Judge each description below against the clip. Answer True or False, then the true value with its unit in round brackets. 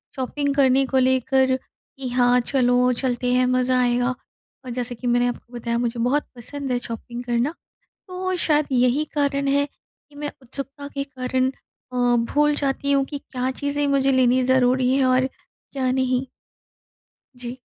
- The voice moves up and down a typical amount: False (2.1 semitones)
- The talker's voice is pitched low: False (260 Hz)